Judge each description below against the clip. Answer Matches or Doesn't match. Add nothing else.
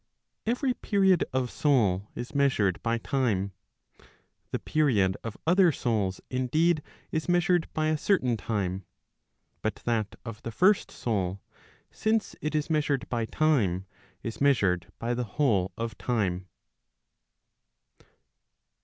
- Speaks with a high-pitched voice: Doesn't match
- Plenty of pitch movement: Matches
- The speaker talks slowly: Matches